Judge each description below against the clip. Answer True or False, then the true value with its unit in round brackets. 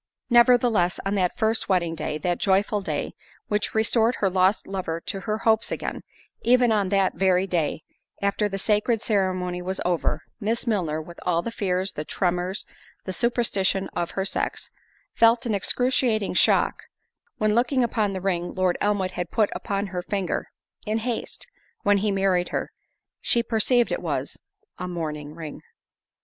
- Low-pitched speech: False (195 Hz)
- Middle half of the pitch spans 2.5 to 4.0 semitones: True (3.5 semitones)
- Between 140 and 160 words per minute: True (155 wpm)